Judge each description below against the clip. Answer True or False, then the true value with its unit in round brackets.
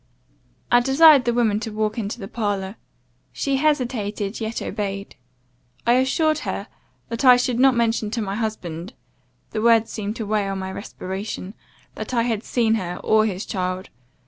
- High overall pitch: True (220 Hz)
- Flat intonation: False (3.3 semitones)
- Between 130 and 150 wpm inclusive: False (170 wpm)